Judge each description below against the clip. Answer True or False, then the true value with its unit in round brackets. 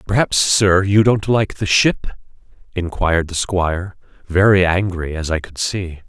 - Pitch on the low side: True (95 Hz)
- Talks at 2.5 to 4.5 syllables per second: True (4.4 syllables/s)